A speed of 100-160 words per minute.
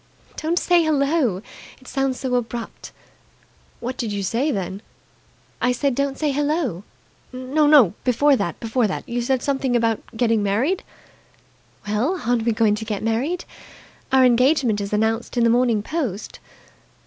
Yes: average, 150 wpm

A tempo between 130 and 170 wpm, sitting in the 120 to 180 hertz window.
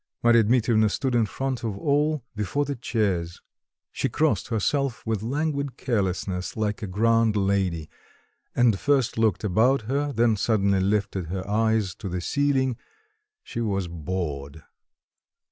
No: average, 140 wpm; low, 110 Hz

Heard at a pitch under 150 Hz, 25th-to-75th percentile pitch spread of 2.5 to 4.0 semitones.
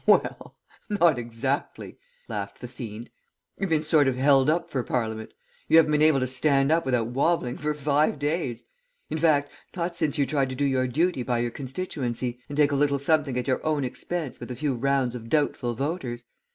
Yes: medium, 140 Hz; average, 3.6 semitones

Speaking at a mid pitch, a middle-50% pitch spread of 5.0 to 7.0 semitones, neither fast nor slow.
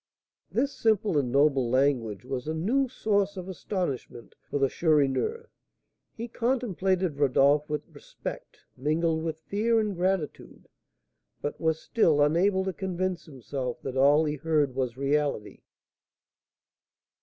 No: medium, 160 Hz; wide, 5.6 semitones; slow, 130 wpm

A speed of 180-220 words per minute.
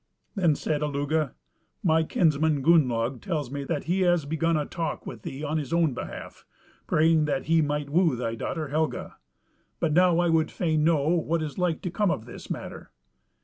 Yes: average, 190 wpm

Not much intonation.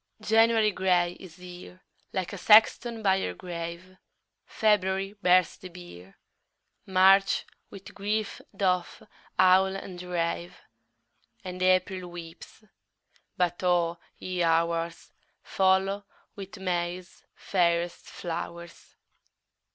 Yes: narrow, 1.9 semitones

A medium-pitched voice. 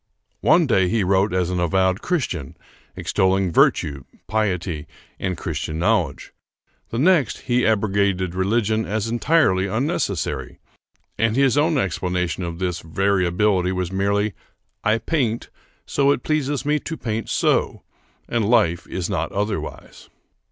No: low, 100 Hz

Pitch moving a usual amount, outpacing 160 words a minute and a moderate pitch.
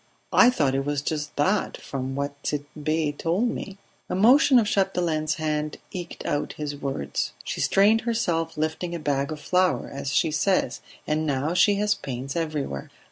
Yes: average, 4.5 semitones; average, 170 wpm; medium, 155 Hz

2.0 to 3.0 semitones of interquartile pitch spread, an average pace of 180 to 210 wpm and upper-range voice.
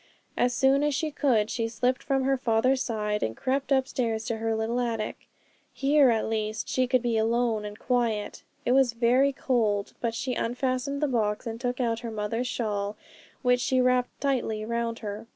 Yes: narrow, 2.6 semitones; average, 190 wpm; high, 240 Hz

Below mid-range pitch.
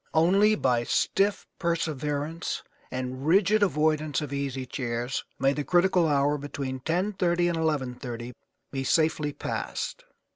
No: medium, 150 Hz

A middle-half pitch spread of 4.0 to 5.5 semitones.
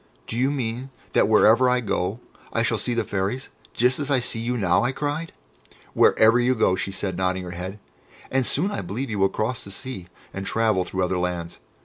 Yes: average, 5.0 semitones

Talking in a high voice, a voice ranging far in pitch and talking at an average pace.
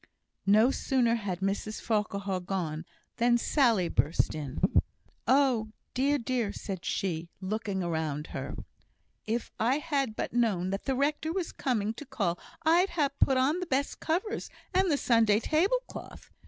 Yes: high, 230 Hz; wide, 6.4 semitones; average, 150 wpm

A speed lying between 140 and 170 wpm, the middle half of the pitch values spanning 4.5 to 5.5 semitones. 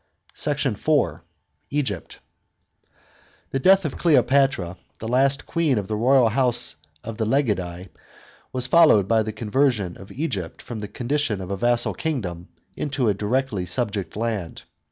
Yes: average, 155 wpm; average, 5.1 semitones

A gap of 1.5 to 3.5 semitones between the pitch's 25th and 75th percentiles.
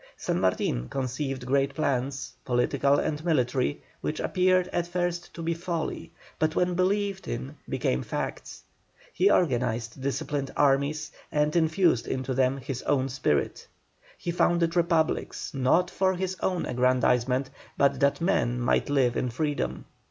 No: average, 4.9 semitones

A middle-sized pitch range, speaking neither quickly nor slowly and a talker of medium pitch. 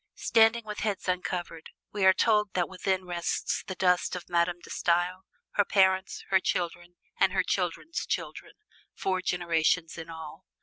No: narrow, 1.7 semitones; average, 160 wpm; medium, 180 Hz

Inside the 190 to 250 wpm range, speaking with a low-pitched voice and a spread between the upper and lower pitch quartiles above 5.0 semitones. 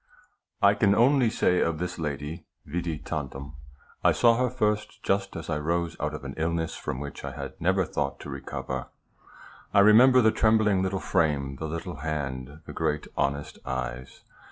No: average, 175 wpm; very low, 80 Hz; wide, 5.6 semitones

